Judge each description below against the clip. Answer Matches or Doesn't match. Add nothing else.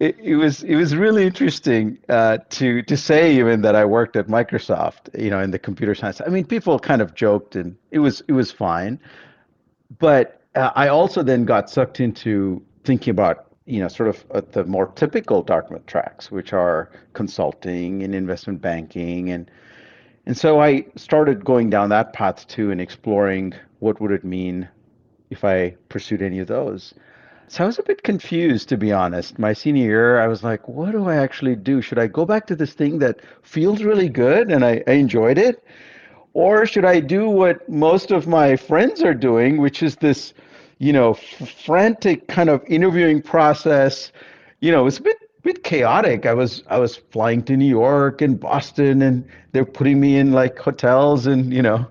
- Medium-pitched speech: Doesn't match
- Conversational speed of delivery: Matches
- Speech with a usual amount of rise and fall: Doesn't match